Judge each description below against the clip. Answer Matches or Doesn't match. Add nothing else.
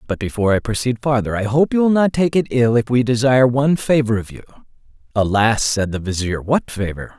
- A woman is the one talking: Doesn't match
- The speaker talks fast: Matches